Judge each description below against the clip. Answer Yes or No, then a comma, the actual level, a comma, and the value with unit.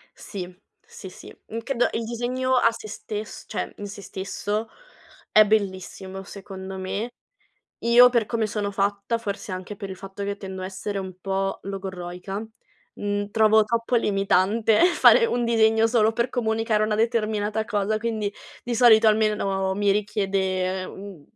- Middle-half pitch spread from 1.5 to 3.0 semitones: Yes, narrow, 2.5 semitones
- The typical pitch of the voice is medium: No, high, 210 Hz